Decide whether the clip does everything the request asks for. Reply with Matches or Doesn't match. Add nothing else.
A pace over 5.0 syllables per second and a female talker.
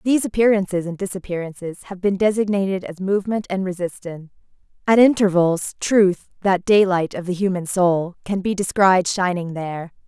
Matches